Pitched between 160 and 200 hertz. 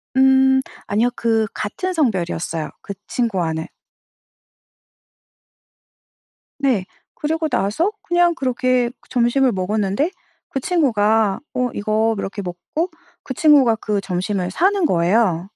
No: high, 230 Hz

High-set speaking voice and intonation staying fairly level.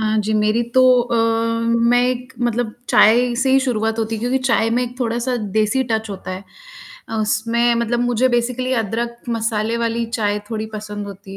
Yes: high, 230 Hz; narrow, 2.0 semitones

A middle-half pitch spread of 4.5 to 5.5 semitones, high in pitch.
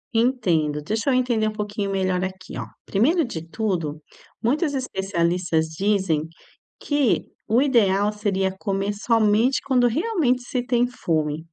Yes: average, 4.8 semitones; high, 210 Hz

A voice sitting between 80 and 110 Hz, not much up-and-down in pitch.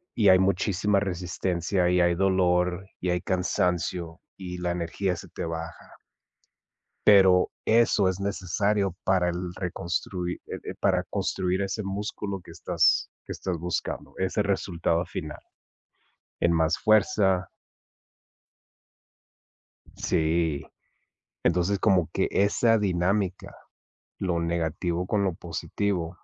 Yes: very low, 90 Hz; narrow, 2.1 semitones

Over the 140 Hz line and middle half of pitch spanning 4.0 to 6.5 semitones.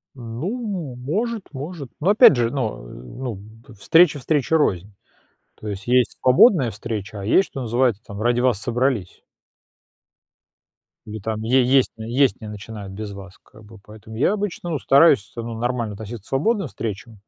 No: low, 120 Hz; average, 4.5 semitones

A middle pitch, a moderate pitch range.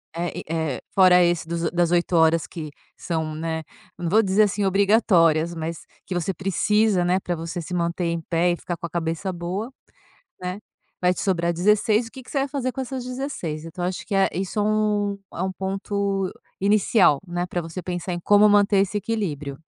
Yes: medium, 180 Hz; average, 3.4 semitones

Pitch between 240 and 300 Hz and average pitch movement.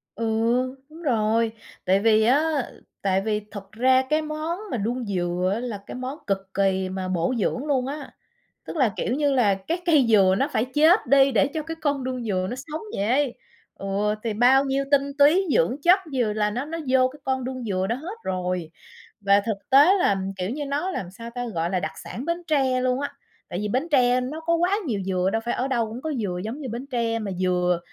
No: high, 245 Hz; wide, 5.9 semitones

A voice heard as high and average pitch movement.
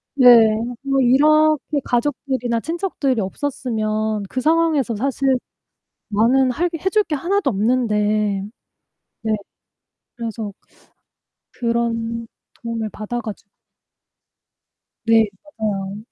Yes: high, 240 Hz; average, 4.2 semitones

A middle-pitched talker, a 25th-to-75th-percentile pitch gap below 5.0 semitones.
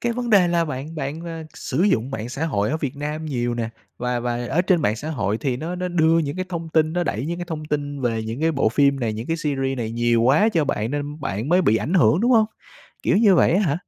No: medium, 150 Hz; wide, 5.5 semitones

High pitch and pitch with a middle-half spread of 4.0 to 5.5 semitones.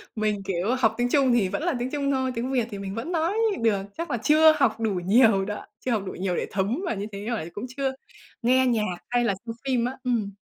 Yes: high, 235 Hz; average, 4.3 semitones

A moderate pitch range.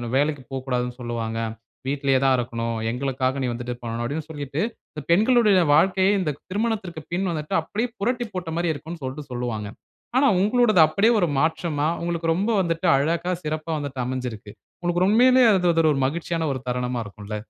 No: wide, 6.1 semitones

